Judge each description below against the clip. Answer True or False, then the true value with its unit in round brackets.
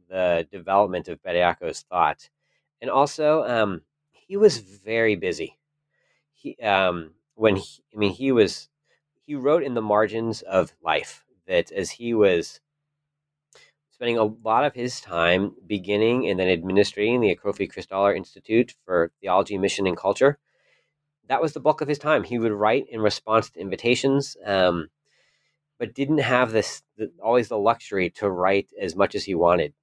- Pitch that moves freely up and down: True (6.7 semitones)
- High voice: False (110 Hz)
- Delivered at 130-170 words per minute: True (160 wpm)